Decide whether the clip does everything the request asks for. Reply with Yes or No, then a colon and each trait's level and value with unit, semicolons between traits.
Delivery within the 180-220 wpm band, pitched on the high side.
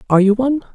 No: fast, 240 wpm; high, 235 Hz